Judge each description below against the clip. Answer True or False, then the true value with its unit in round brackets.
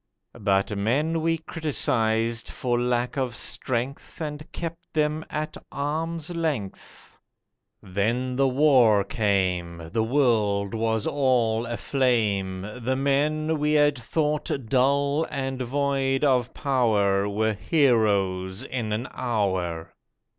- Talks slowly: True (110 wpm)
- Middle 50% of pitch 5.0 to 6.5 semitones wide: True (5.3 semitones)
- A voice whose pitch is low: True (125 Hz)